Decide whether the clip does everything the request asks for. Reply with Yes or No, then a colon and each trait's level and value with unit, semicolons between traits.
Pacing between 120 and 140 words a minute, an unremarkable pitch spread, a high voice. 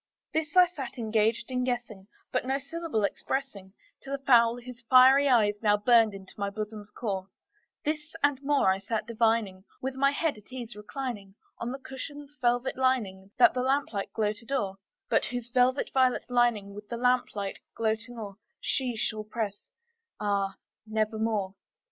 No: average, 160 wpm; average, 3.9 semitones; high, 235 Hz